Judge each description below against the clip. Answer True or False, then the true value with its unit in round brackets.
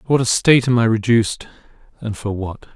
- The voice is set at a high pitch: False (115 Hz)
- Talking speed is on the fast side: True (220 wpm)